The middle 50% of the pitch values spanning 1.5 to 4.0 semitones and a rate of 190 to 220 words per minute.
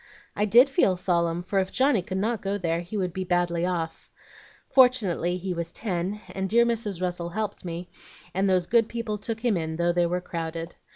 Yes: average, 3.6 semitones; fast, 205 wpm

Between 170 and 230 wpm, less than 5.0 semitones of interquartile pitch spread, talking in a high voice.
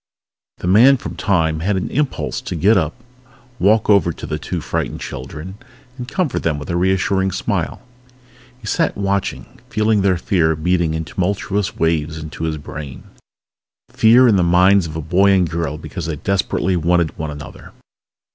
No: average, 175 wpm; average, 3.8 semitones; very low, 90 Hz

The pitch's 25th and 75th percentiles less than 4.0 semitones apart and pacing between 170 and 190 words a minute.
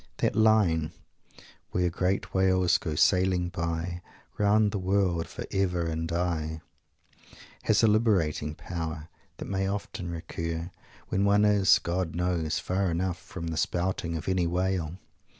No: narrow, 2.6 semitones; average, 140 wpm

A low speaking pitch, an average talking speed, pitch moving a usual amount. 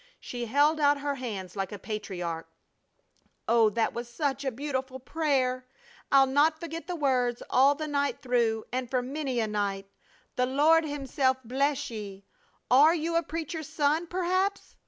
No: very high, 265 Hz; average, 160 wpm; average, 4.2 semitones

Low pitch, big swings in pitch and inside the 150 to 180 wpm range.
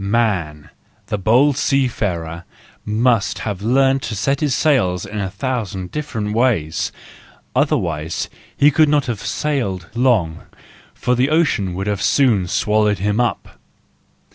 No: low, 110 Hz; wide, 5.7 semitones; slow, 135 wpm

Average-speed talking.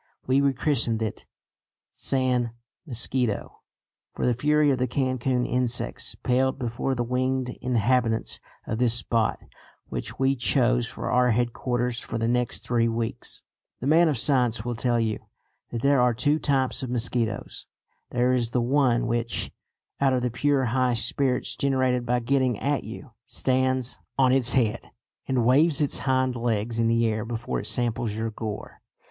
Yes: average, 160 wpm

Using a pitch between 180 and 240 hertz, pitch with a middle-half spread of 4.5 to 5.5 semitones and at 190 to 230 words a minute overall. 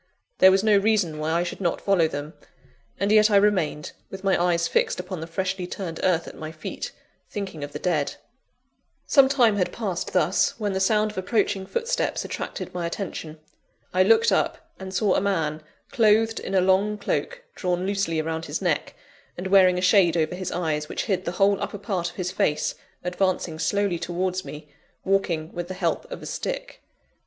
No: medium, 185 Hz; average, 3.2 semitones; average, 195 wpm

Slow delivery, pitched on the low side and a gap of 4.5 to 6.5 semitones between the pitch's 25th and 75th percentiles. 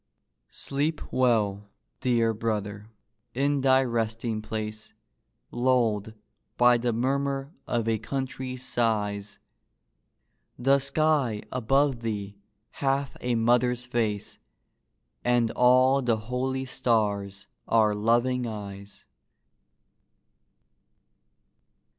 No: slow, 85 wpm; low, 120 Hz; average, 3.2 semitones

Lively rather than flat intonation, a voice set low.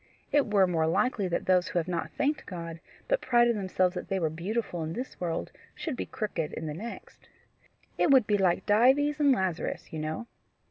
No: wide, 6.2 semitones; high, 190 Hz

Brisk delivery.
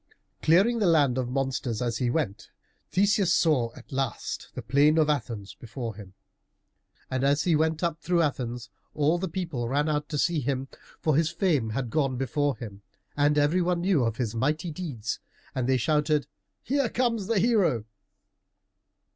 No: average, 170 wpm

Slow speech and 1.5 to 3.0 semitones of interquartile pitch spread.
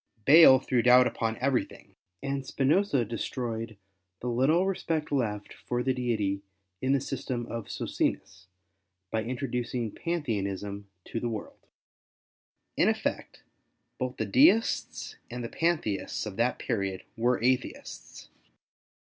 No: slow, 125 wpm; average, 3.6 semitones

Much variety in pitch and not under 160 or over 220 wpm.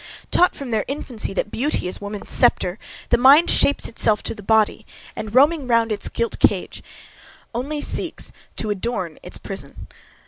No: average, 4.5 semitones; average, 165 wpm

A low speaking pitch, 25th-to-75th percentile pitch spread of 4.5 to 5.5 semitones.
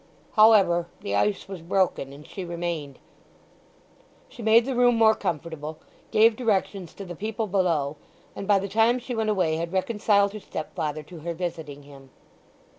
No: medium, 185 Hz; average, 5.2 semitones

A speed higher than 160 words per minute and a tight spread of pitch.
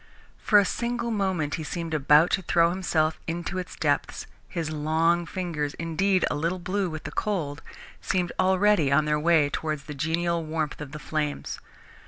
No: average, 175 wpm; average, 3.2 semitones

